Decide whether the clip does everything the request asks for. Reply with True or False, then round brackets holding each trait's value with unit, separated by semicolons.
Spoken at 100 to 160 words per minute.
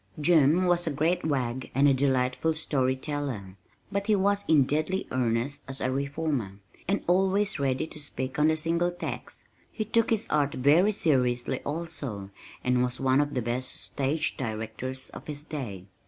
False (170 wpm)